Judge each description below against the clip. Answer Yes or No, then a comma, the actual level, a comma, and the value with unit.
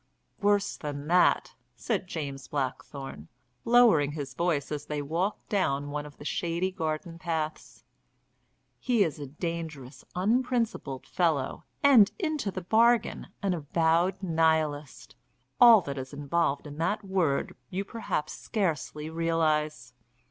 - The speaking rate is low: Yes, slow, 125 wpm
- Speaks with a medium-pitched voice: Yes, medium, 165 Hz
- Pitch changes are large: No, average, 4.9 semitones